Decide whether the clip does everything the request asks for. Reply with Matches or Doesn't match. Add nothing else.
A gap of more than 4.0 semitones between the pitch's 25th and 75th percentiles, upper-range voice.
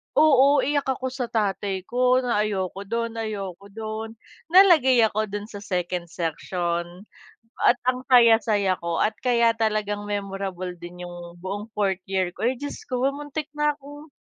Matches